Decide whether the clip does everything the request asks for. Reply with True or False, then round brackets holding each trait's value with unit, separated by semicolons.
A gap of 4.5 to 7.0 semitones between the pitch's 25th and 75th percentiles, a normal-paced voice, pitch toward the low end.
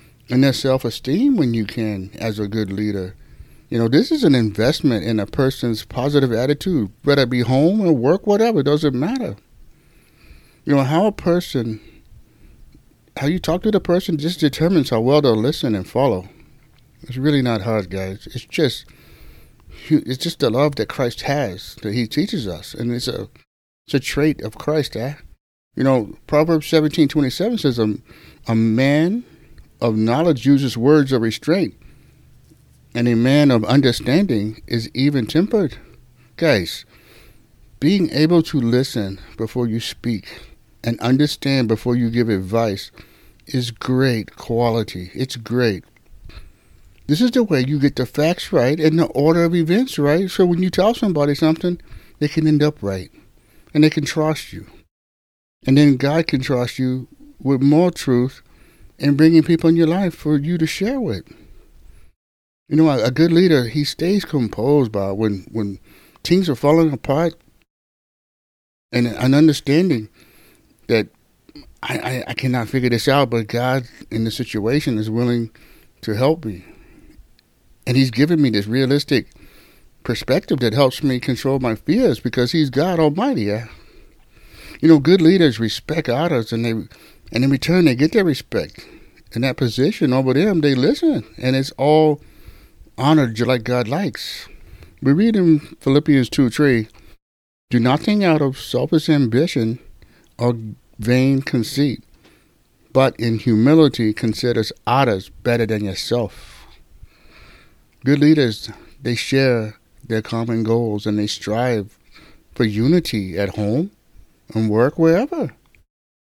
True (5.2 semitones; 150 wpm; 130 Hz)